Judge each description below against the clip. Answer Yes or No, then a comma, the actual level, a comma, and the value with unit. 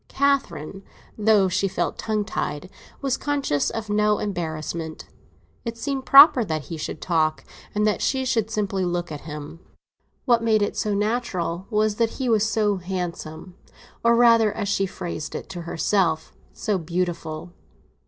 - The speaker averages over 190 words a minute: No, average, 155 wpm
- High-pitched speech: Yes, high, 200 Hz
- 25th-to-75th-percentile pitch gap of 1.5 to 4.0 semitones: No, average, 4.8 semitones